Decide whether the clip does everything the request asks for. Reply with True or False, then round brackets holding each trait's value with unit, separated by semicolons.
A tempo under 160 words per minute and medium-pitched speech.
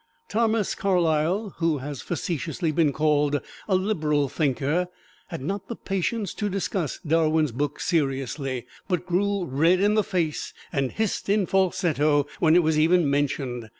True (150 wpm; 165 Hz)